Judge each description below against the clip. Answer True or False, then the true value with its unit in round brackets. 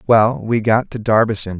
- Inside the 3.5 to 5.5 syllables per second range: True (4.8 syllables/s)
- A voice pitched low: True (110 Hz)